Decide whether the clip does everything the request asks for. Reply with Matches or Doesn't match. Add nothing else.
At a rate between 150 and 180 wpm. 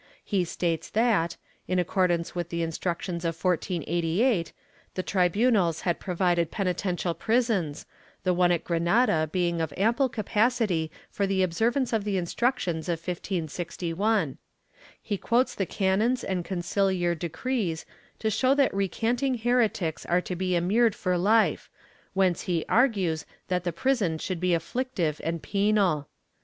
Doesn't match